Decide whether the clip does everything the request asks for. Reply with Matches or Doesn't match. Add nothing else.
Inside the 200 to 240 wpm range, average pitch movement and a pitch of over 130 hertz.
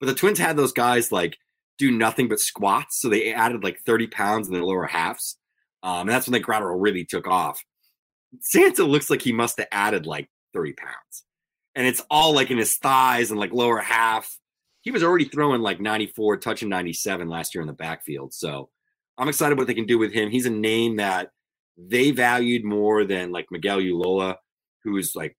Doesn't match